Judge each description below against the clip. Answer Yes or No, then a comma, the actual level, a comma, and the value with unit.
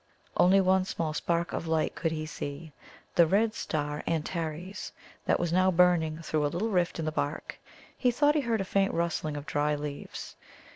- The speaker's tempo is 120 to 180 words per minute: No, average, 190 wpm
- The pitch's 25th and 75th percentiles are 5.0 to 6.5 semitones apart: No, average, 3.3 semitones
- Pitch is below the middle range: No, medium, 170 Hz